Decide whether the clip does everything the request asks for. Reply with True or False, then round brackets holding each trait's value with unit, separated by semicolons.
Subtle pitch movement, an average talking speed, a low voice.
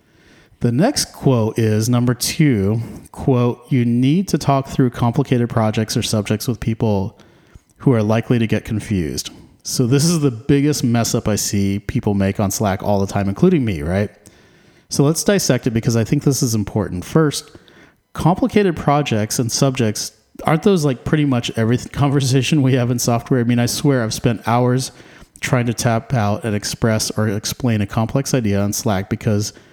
False (4.4 semitones; 180 wpm; 120 Hz)